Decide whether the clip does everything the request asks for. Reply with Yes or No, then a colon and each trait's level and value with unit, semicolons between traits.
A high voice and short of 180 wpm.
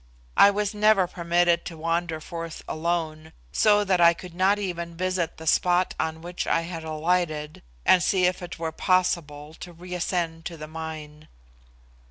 No: medium, 170 Hz; average, 165 wpm